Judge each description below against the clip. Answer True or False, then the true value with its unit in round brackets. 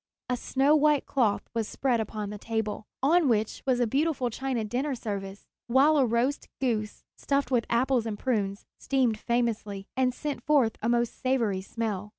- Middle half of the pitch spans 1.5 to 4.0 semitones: True (3.7 semitones)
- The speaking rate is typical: True (170 wpm)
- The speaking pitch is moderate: False (235 Hz)